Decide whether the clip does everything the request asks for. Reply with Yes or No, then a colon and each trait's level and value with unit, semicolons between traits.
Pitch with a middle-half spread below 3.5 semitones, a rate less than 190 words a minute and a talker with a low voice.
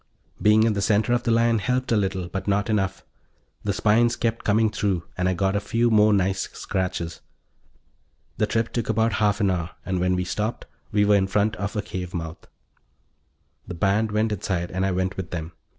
No: average, 2.8 semitones; fast, 205 wpm; low, 100 Hz